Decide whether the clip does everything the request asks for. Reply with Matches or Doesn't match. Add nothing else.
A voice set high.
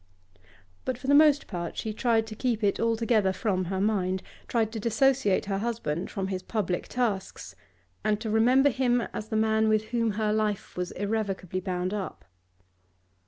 Matches